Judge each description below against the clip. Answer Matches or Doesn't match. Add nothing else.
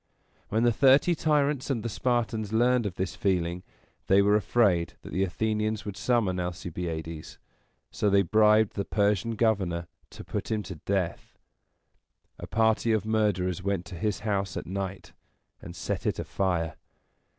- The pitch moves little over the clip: Doesn't match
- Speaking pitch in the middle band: Doesn't match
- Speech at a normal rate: Matches